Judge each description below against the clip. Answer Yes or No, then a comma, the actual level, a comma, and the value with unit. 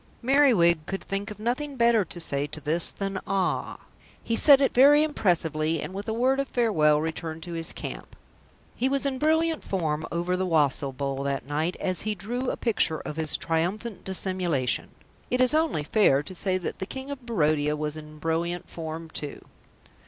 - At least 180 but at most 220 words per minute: Yes, average, 190 wpm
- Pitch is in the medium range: Yes, medium, 180 Hz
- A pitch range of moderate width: No, wide, 7.1 semitones